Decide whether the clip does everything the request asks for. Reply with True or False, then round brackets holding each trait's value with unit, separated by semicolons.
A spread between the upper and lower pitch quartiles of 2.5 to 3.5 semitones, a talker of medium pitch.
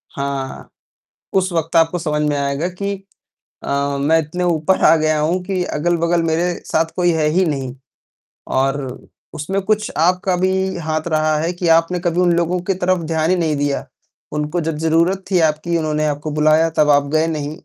True (2.8 semitones; 160 Hz)